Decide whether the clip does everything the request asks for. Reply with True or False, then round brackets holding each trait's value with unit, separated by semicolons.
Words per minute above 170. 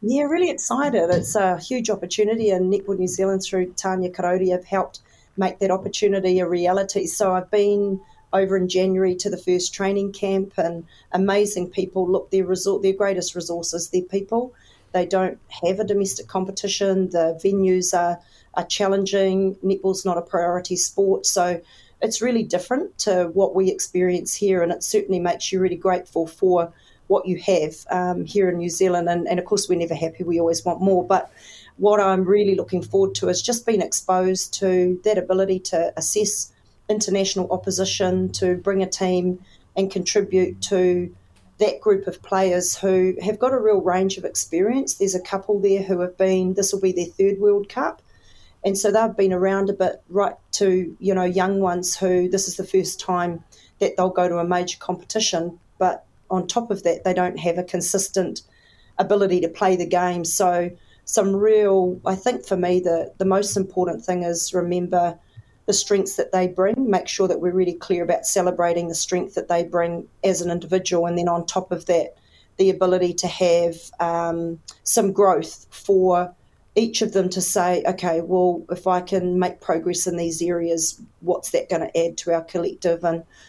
True (185 wpm)